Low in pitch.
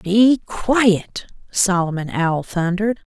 No: high, 190 Hz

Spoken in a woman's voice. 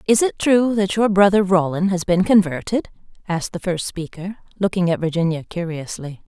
Yes: female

